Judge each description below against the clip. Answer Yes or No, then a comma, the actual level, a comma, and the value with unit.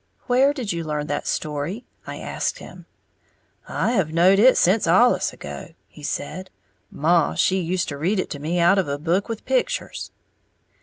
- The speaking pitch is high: No, medium, 180 Hz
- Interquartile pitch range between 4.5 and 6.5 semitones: Yes, average, 5.3 semitones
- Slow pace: No, average, 175 wpm